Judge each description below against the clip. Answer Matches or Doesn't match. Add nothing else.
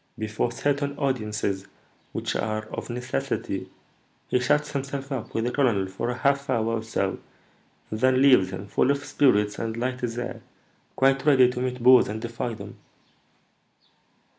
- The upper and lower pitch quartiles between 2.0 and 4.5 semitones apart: Matches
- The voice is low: Matches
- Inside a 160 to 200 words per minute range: Matches